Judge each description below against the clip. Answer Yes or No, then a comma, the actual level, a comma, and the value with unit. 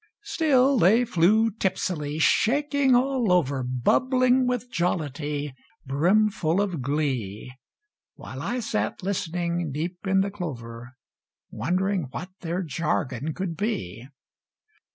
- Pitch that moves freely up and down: Yes, wide, 7.1 semitones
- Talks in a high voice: No, medium, 180 Hz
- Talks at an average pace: No, slow, 110 wpm